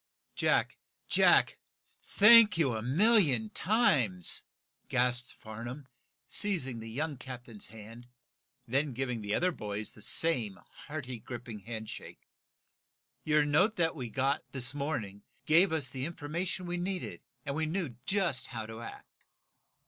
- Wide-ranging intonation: Yes, wide, 6.1 semitones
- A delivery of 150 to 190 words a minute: No, slow, 135 wpm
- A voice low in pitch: Yes, low, 130 Hz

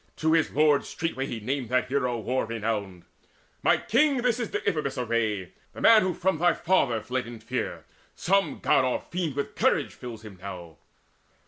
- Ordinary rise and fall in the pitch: No, wide, 7.0 semitones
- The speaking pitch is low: Yes, low, 130 Hz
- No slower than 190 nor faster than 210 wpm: No, average, 180 wpm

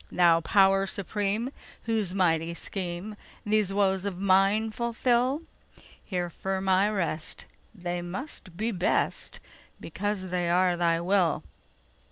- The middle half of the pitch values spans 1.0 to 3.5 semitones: Yes, average, 3.0 semitones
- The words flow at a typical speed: No, slow, 105 wpm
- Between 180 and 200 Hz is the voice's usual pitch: Yes, high, 190 Hz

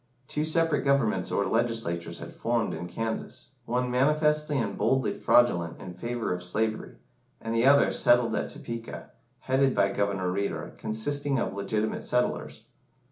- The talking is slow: No, average, 145 wpm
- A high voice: No, low, 115 Hz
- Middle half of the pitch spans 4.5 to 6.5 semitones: Yes, average, 5.1 semitones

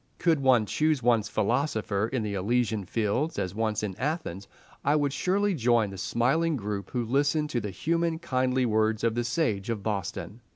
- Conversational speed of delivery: Yes, average, 180 wpm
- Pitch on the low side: Yes, low, 120 Hz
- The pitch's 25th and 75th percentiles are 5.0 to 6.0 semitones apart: Yes, wide, 5.5 semitones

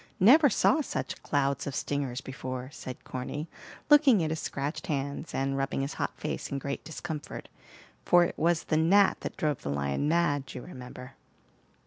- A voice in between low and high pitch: Yes, medium, 145 Hz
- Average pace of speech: Yes, average, 170 wpm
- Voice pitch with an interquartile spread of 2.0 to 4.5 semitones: Yes, average, 4.0 semitones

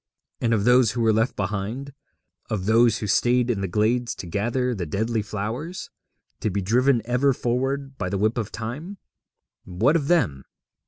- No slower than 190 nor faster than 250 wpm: No, average, 175 wpm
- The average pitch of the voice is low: Yes, low, 115 Hz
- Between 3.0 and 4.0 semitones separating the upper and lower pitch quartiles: Yes, average, 3.4 semitones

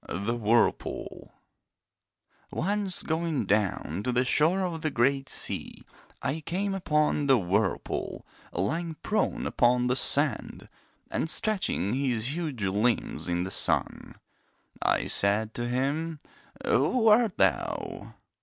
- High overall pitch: No, low, 135 Hz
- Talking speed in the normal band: No, slow, 120 wpm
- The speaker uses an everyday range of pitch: No, wide, 7.2 semitones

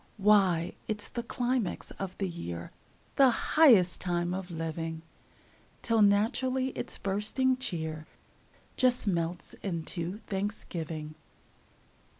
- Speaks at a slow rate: Yes, slow, 105 wpm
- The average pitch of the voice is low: No, high, 190 Hz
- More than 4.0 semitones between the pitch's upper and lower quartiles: Yes, average, 5.1 semitones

